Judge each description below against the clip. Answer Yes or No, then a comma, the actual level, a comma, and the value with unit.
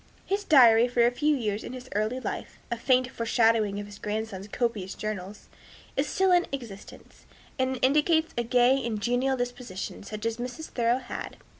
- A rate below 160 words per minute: No, average, 175 wpm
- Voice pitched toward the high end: Yes, high, 240 Hz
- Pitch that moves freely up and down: No, average, 3.4 semitones